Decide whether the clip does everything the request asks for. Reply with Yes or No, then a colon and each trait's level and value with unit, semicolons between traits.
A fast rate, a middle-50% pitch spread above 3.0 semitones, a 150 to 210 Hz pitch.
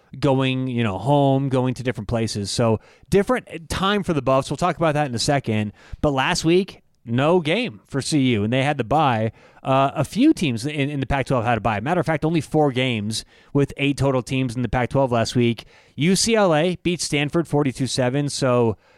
No: fast, 215 wpm; average, 4.0 semitones; low, 135 Hz